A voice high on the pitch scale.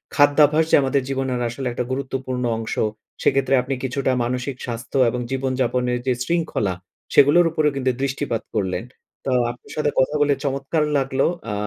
No: low, 135 Hz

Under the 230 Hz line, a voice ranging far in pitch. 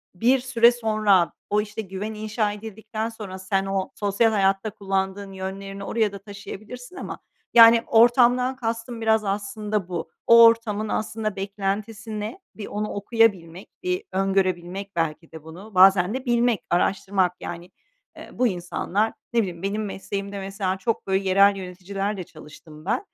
No: high, 200 Hz; narrow, 2.6 semitones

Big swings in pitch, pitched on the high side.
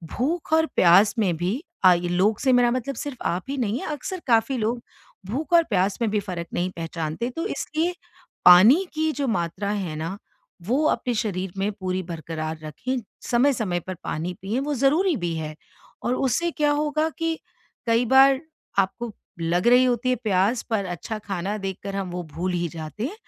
Yes: wide, 6.7 semitones; high, 215 Hz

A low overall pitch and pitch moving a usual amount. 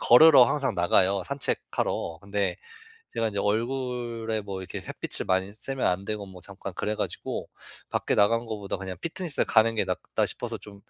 Yes: low, 105 Hz; average, 3.6 semitones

